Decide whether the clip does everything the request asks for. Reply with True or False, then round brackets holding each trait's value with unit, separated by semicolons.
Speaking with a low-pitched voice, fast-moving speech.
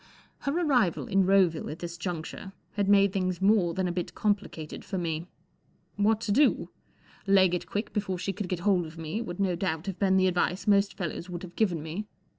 False (190 Hz; 215 wpm)